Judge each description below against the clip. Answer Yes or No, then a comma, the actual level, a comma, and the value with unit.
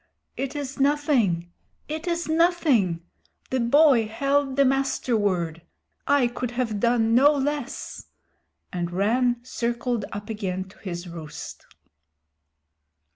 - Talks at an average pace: No, slow, 120 wpm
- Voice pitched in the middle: No, high, 240 Hz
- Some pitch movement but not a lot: No, wide, 5.7 semitones